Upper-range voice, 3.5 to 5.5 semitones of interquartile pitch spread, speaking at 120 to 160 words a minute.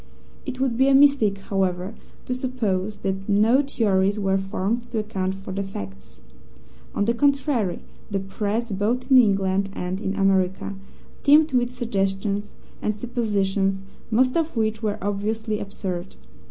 Yes: high, 205 Hz; average, 3.8 semitones; average, 145 wpm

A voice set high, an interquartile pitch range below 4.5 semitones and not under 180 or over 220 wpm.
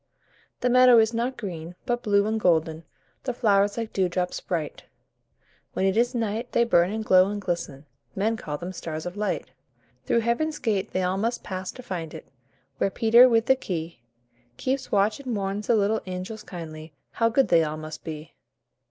No: high, 200 Hz; average, 4.9 semitones; average, 185 wpm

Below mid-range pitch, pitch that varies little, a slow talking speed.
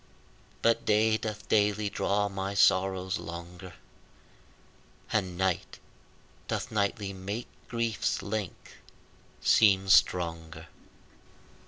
Yes: low, 100 Hz; narrow, 2.2 semitones; slow, 85 wpm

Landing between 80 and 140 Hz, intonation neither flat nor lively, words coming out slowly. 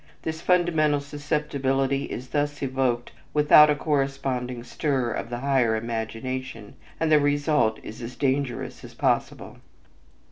Yes: low, 135 Hz; average, 3.0 semitones; slow, 130 wpm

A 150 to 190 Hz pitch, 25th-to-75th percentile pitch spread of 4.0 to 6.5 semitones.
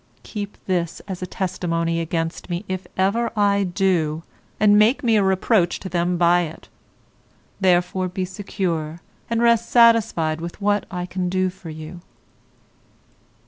No: medium, 185 Hz; average, 3.0 semitones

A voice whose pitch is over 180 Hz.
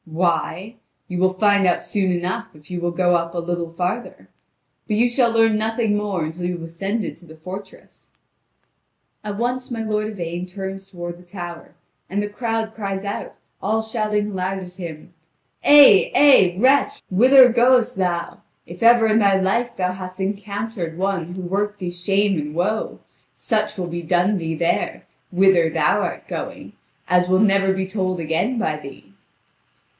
Yes: high, 190 Hz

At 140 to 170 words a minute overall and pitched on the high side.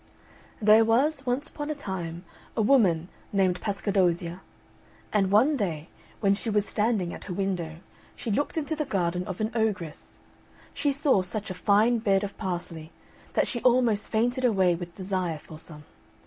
Yes: average, 165 wpm; high, 200 Hz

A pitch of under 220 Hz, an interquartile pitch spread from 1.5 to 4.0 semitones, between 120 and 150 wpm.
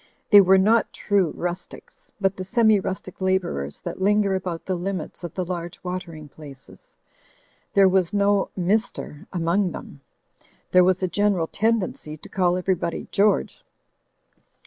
Yes: medium, 185 Hz; narrow, 2.5 semitones; average, 145 wpm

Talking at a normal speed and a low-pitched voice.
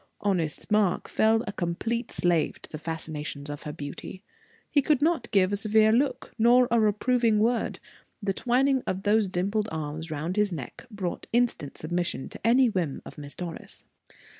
No: average, 170 wpm; high, 200 Hz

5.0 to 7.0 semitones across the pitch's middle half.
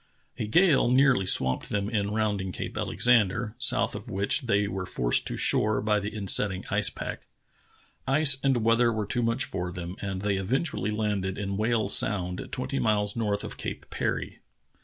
No: average, 3.2 semitones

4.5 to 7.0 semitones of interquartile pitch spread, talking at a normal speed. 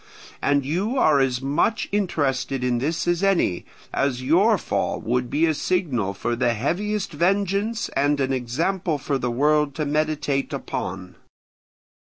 Yes: wide, 5.5 semitones; average, 150 wpm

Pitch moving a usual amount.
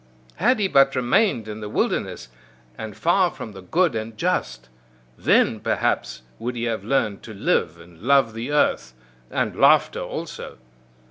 No: wide, 5.7 semitones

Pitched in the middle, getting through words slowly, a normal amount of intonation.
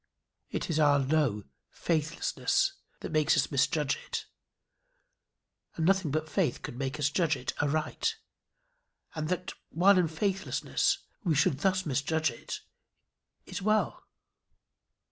Yes: medium, 155 Hz; slow, 125 wpm; average, 4.0 semitones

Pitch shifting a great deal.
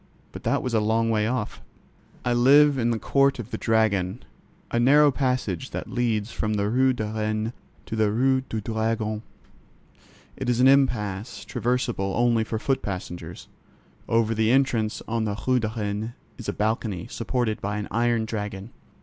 No: narrow, 2.6 semitones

